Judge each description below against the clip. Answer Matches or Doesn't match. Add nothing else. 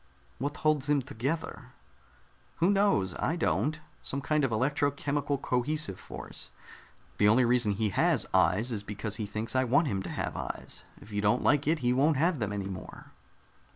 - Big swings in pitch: Matches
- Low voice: Matches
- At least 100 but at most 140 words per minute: Doesn't match